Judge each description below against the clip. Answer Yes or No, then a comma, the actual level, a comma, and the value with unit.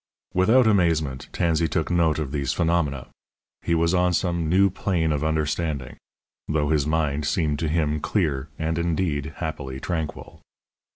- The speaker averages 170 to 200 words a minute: No, average, 150 wpm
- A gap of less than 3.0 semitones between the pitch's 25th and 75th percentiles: Yes, narrow, 2.4 semitones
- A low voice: Yes, very low, 80 Hz